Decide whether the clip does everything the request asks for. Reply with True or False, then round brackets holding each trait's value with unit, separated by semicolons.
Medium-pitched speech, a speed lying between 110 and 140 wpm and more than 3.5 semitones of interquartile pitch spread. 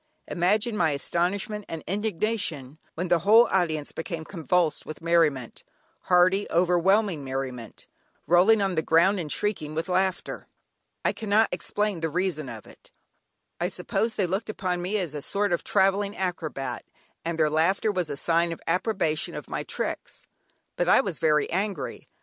False (175 Hz; 160 wpm; 3.9 semitones)